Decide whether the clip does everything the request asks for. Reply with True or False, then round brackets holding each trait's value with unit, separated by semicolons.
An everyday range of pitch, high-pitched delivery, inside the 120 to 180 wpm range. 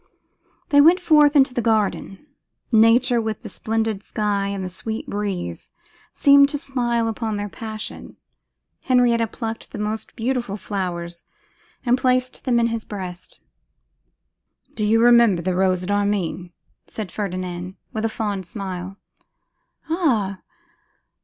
True (3.7 semitones; 220 Hz; 135 wpm)